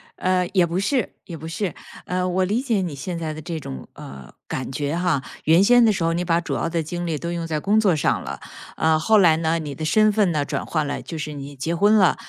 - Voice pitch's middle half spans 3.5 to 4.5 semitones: No, average, 3.1 semitones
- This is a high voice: No, medium, 170 Hz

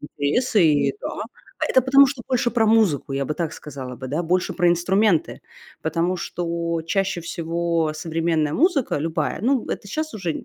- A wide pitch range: Yes, wide, 5.7 semitones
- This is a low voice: No, medium, 170 Hz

